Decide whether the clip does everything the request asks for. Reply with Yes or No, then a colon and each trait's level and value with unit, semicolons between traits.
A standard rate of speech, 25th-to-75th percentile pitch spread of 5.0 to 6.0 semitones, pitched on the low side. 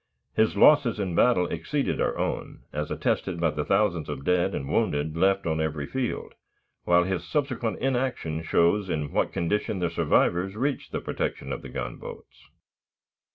Yes: average, 160 wpm; wide, 5.4 semitones; very low, 90 Hz